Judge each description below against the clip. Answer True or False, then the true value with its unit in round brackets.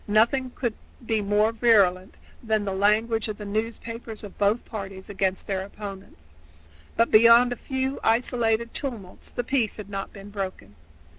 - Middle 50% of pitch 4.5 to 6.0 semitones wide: False (2.7 semitones)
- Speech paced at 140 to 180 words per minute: True (155 wpm)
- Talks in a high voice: True (215 Hz)